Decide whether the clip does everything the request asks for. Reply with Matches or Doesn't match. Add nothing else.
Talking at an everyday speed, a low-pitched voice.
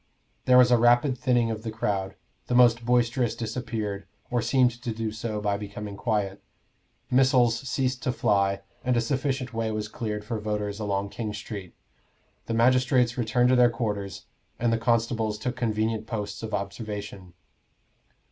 Matches